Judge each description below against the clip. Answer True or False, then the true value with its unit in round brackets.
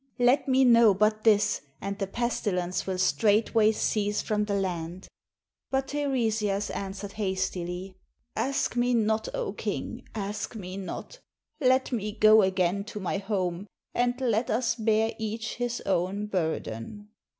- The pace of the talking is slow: False (145 wpm)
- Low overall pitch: False (210 Hz)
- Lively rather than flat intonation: False (3.2 semitones)